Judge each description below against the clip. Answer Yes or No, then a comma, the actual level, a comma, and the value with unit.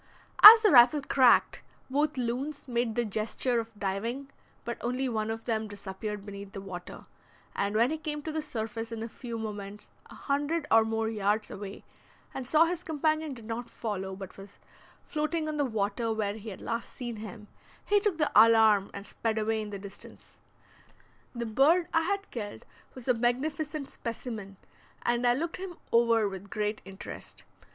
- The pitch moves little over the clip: No, average, 5.0 semitones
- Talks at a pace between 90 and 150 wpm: No, average, 180 wpm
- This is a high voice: Yes, high, 230 Hz